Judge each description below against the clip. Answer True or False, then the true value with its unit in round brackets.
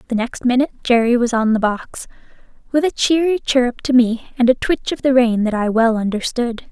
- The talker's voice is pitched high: True (245 Hz)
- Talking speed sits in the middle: False (215 wpm)